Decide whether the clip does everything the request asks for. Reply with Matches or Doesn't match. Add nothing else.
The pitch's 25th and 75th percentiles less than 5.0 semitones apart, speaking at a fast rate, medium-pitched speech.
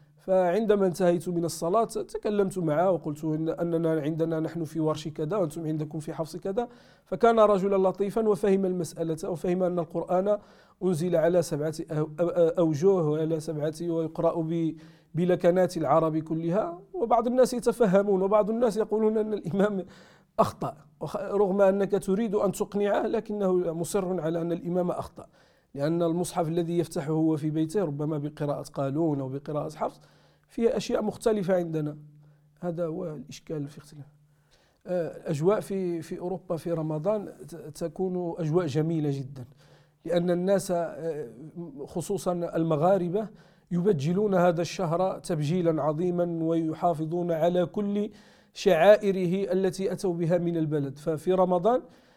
Doesn't match